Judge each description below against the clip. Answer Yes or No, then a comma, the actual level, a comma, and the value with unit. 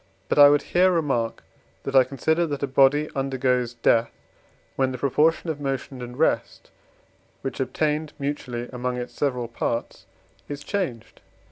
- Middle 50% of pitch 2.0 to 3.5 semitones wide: Yes, average, 2.9 semitones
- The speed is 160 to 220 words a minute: No, average, 150 wpm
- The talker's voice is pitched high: No, low, 135 Hz